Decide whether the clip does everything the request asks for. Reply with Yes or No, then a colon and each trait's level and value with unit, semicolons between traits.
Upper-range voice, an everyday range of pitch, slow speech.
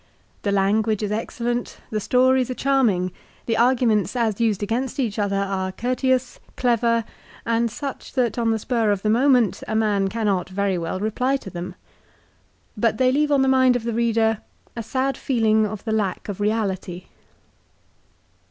No: high, 225 Hz; average, 3.4 semitones; average, 170 wpm